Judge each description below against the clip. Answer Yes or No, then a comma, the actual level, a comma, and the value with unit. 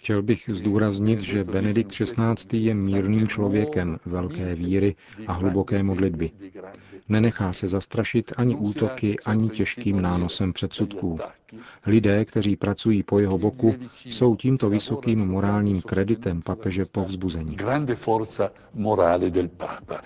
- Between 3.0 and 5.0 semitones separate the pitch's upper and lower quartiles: No, narrow, 2.5 semitones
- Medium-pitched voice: No, low, 100 Hz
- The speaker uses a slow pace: Yes, slow, 110 wpm